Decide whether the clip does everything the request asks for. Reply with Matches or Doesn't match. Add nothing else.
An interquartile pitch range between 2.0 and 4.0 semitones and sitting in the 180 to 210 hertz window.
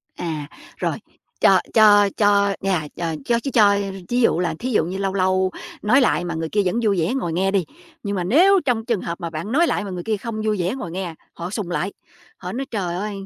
Matches